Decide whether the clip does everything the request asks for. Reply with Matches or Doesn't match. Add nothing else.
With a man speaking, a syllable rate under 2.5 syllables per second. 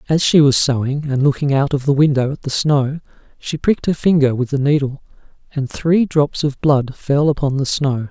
Doesn't match